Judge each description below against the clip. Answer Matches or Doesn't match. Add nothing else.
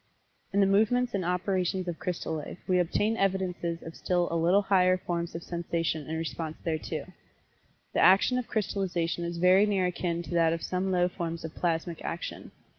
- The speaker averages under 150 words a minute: Doesn't match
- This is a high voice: Doesn't match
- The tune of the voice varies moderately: Doesn't match